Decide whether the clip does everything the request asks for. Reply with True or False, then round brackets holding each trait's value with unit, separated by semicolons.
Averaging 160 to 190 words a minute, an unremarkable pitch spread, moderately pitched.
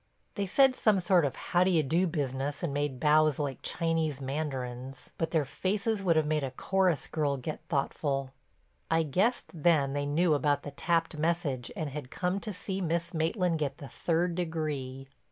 True (180 wpm; 3.7 semitones; 155 Hz)